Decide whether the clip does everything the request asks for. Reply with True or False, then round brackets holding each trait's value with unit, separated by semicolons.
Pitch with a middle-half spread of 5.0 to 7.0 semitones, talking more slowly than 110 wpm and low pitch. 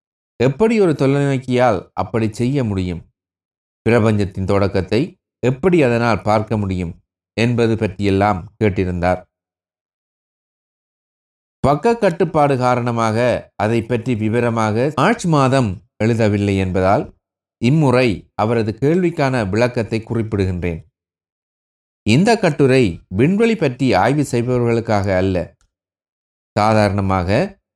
True (5.3 semitones; 80 wpm; 110 Hz)